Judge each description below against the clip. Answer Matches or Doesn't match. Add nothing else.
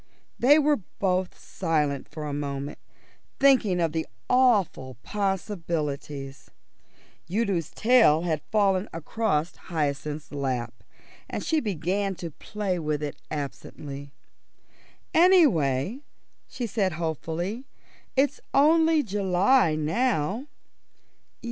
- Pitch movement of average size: Doesn't match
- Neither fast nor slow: Doesn't match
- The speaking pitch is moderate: Matches